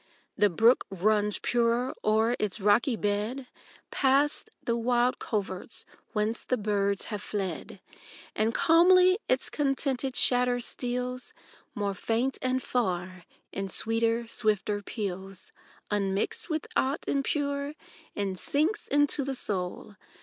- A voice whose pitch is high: Yes, high, 230 Hz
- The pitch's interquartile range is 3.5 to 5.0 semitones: Yes, average, 4.3 semitones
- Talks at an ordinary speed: No, slow, 120 wpm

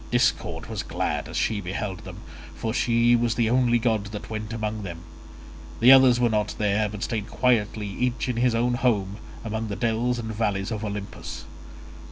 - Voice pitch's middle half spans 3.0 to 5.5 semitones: No, narrow, 2.4 semitones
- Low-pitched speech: Yes, low, 110 Hz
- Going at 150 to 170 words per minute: No, average, 185 wpm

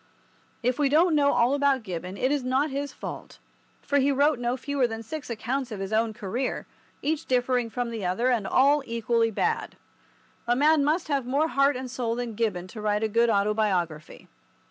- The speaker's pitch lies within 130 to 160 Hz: No, high, 245 Hz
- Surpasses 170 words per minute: Yes, average, 195 wpm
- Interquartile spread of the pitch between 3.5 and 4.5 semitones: Yes, average, 4.2 semitones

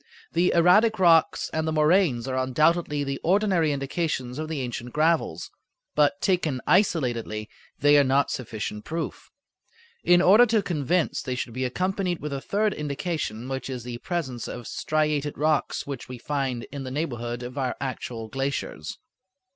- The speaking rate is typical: Yes, average, 160 wpm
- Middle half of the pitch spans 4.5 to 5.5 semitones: Yes, average, 4.8 semitones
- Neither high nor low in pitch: Yes, medium, 145 Hz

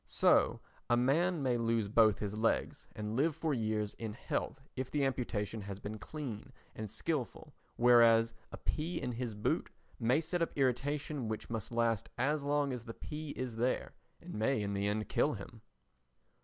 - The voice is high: No, low, 120 Hz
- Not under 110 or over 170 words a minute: No, average, 180 wpm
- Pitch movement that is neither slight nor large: Yes, average, 4.3 semitones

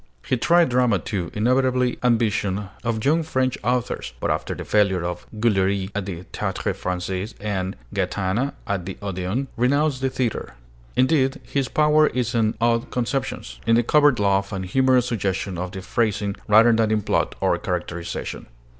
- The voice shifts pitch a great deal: No, average, 4.8 semitones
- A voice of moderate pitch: No, low, 110 Hz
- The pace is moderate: Yes, average, 165 wpm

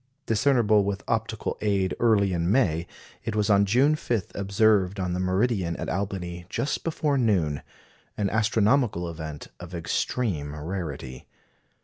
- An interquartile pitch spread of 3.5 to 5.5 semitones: Yes, average, 4.1 semitones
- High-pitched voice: No, low, 100 Hz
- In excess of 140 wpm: No, slow, 135 wpm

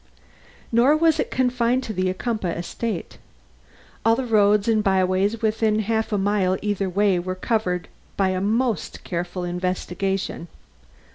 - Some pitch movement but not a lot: Yes, average, 3.5 semitones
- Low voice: No, high, 205 Hz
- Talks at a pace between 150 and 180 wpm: No, average, 140 wpm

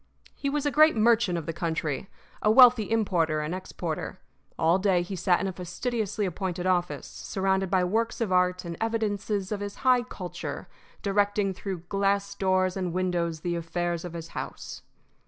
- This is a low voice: No, medium, 185 Hz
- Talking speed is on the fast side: No, average, 175 wpm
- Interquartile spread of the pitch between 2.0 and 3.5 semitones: Yes, average, 3.0 semitones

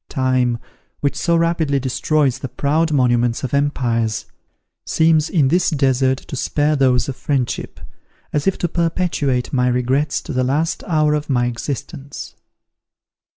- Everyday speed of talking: Yes, average, 145 wpm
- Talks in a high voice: No, medium, 140 Hz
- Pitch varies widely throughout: No, average, 3.4 semitones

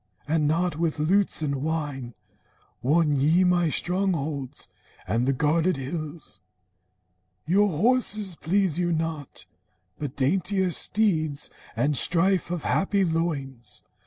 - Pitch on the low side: No, medium, 160 Hz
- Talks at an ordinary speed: No, slow, 115 wpm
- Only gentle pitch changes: No, average, 3.8 semitones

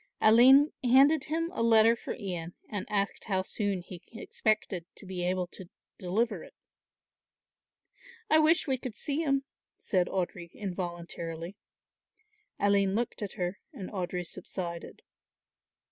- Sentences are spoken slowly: Yes, slow, 130 wpm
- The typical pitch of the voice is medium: No, high, 200 Hz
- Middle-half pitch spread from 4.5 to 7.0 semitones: Yes, average, 5.0 semitones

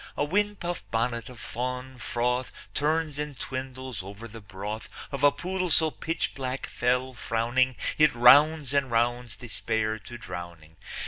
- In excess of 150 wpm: No, average, 140 wpm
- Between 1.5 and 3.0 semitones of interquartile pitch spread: No, average, 3.9 semitones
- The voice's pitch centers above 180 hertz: No, low, 125 Hz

